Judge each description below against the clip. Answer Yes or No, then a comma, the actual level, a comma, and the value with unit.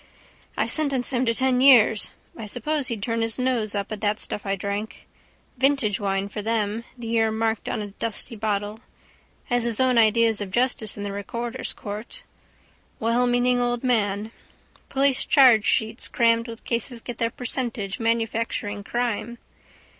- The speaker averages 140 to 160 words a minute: Yes, average, 155 wpm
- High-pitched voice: Yes, high, 230 Hz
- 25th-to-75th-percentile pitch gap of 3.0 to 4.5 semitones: No, narrow, 2.6 semitones